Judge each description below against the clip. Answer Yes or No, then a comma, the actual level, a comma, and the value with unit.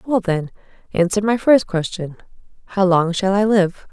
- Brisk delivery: No, average, 170 wpm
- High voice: Yes, high, 195 Hz